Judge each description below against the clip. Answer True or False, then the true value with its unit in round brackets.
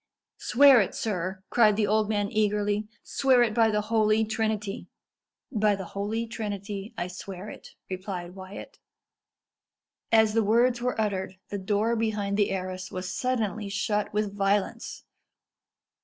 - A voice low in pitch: False (210 Hz)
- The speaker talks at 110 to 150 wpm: True (140 wpm)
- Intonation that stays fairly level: True (2.0 semitones)